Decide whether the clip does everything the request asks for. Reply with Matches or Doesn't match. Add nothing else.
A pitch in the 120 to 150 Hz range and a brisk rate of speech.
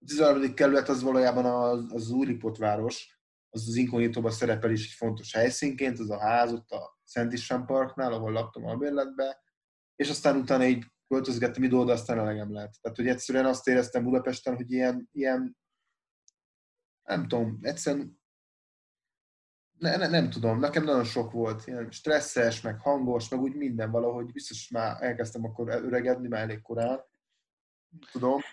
Matches